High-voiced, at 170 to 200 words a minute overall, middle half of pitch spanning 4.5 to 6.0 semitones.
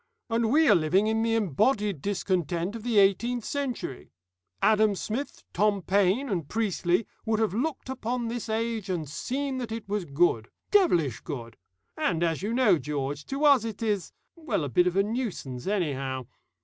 Yes: high, 205 Hz; average, 175 wpm; average, 5.3 semitones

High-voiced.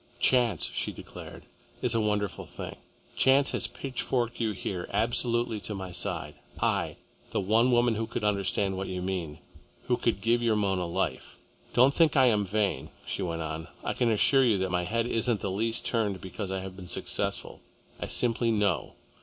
No: low, 105 Hz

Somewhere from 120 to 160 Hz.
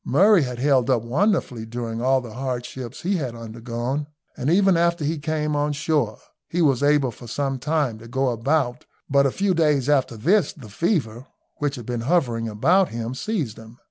Yes: low, 135 Hz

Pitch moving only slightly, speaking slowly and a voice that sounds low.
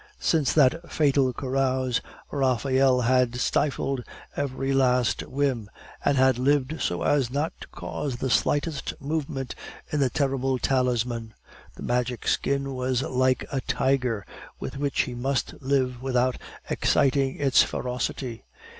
Yes: narrow, 1.6 semitones; slow, 130 wpm; low, 130 Hz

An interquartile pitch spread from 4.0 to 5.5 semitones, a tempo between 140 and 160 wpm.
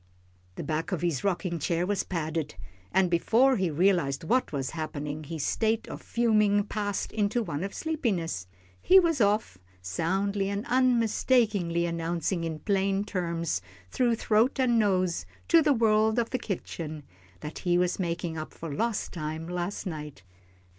Yes: average, 4.9 semitones; average, 155 wpm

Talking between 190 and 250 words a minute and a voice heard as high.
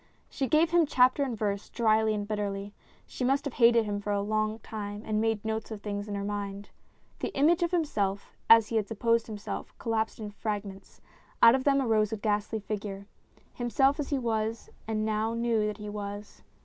Yes: average, 200 wpm; high, 215 Hz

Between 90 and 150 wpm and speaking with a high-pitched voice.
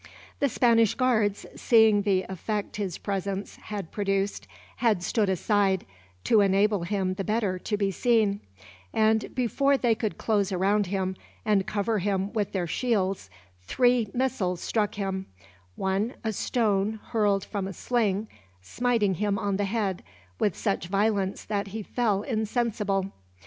Yes: average, 145 wpm; high, 205 Hz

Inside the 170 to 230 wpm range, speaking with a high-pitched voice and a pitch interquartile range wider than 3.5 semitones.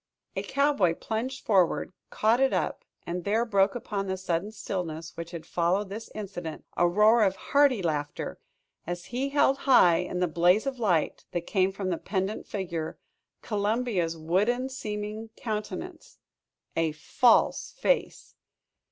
No: average, 145 wpm; high, 200 Hz; average, 4.7 semitones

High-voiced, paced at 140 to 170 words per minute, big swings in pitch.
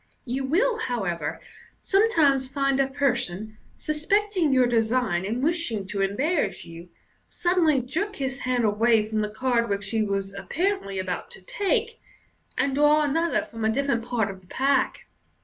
Yes: very high, 255 Hz; average, 155 wpm; wide, 6.1 semitones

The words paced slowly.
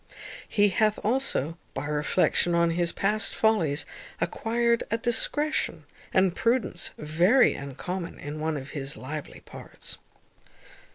Yes: slow, 120 wpm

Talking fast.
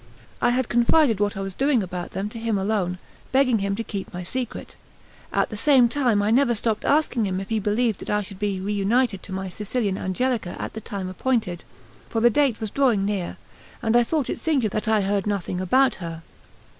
Yes: fast, 215 wpm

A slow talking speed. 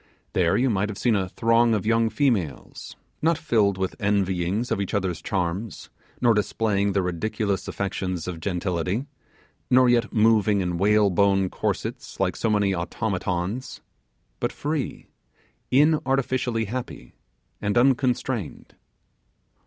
Yes: slow, 125 wpm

